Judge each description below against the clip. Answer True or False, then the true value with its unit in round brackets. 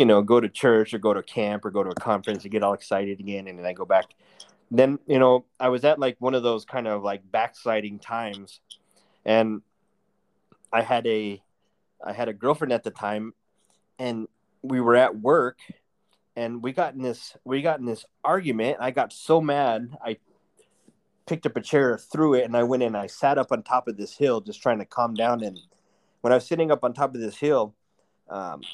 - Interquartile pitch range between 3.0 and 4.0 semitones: True (3.4 semitones)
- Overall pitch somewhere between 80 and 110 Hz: False (120 Hz)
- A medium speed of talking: False (220 wpm)